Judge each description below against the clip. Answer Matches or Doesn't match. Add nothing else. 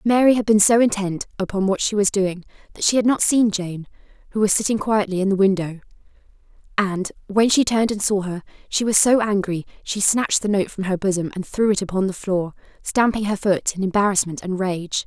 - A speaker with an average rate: Doesn't match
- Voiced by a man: Doesn't match